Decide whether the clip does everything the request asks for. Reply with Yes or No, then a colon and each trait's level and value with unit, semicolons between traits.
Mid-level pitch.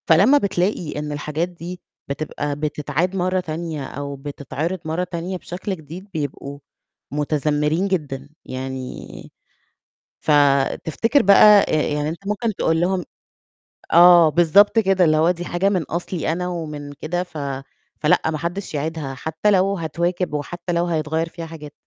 Yes: medium, 165 Hz